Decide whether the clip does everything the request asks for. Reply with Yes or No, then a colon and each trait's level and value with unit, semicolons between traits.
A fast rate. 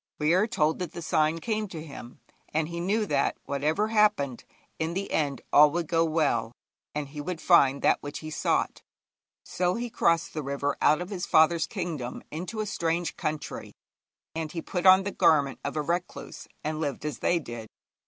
No: average, 195 wpm